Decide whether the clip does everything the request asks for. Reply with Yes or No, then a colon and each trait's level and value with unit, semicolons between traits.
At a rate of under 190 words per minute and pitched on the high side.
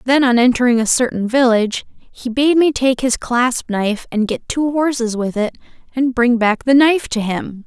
No: fast, 205 wpm; high, 245 Hz